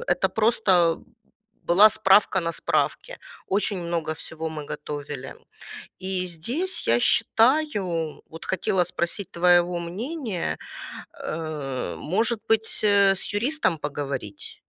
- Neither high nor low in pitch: Yes, medium, 180 Hz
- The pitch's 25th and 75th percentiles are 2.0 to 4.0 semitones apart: No, average, 4.6 semitones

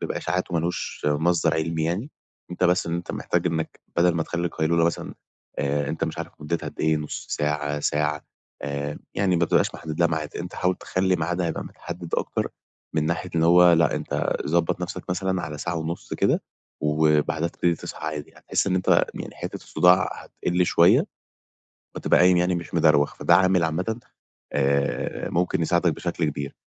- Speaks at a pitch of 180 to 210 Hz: No, very low, 85 Hz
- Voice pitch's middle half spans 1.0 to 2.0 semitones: No, narrow, 2.5 semitones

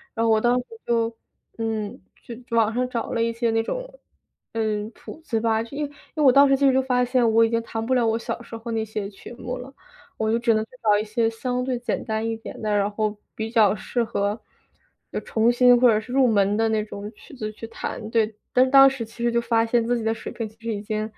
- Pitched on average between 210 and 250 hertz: Yes, high, 230 Hz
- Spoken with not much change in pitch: Yes, narrow, 2.1 semitones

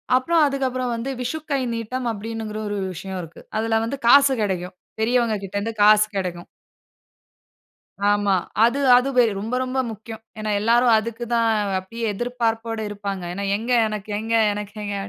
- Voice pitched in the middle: No, high, 225 Hz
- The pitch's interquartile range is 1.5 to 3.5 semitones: Yes, average, 3.0 semitones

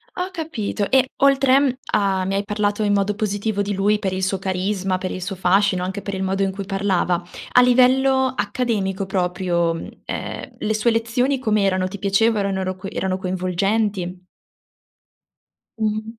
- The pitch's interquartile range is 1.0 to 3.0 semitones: Yes, narrow, 2.6 semitones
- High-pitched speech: Yes, high, 200 Hz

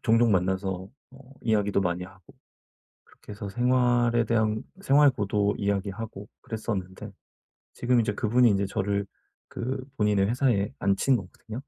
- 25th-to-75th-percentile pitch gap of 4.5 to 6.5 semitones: No, average, 3.4 semitones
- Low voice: Yes, low, 105 Hz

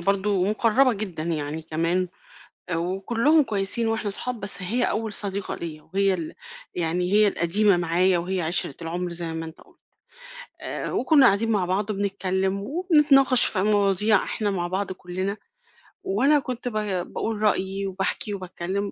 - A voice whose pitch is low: No, high, 195 Hz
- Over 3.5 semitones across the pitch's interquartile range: No, average, 3.2 semitones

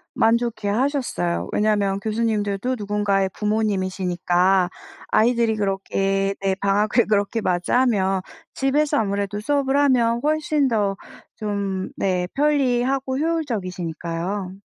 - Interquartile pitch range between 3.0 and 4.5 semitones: Yes, average, 4.1 semitones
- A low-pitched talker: No, high, 210 Hz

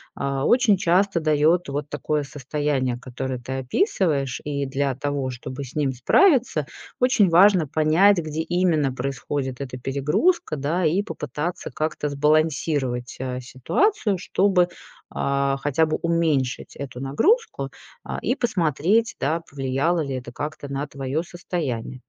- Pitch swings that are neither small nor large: Yes, average, 4.3 semitones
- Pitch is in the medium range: Yes, medium, 150 Hz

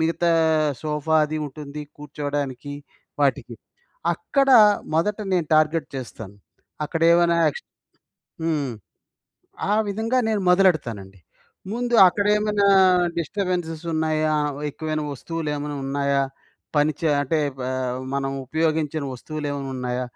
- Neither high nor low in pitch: Yes, medium, 155 Hz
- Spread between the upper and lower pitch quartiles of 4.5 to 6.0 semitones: No, average, 3.1 semitones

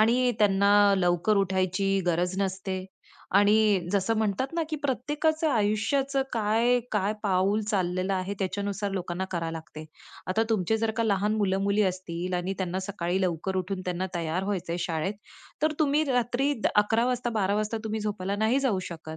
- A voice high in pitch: Yes, high, 200 Hz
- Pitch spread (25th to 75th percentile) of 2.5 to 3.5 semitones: Yes, average, 3.0 semitones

